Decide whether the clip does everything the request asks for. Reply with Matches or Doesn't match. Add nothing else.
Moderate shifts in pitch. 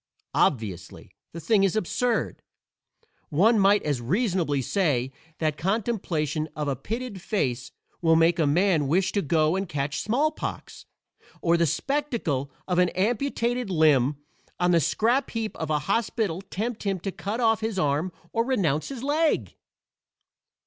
Doesn't match